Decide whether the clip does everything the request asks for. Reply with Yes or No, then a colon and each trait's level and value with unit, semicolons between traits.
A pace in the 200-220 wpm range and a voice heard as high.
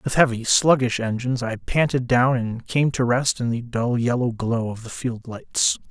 No: fast, 205 wpm; low, 120 Hz